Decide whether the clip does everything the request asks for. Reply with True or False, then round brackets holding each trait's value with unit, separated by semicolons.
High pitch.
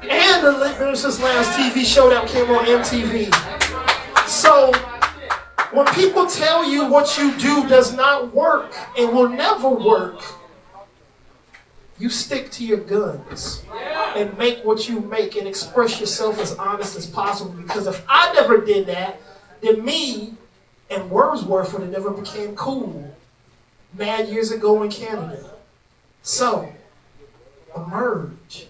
True (230 Hz)